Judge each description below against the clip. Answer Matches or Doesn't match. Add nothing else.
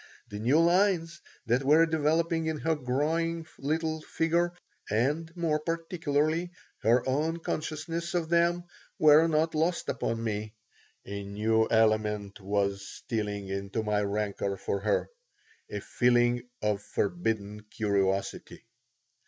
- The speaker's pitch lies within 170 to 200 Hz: Doesn't match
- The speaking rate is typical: Doesn't match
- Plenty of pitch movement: Matches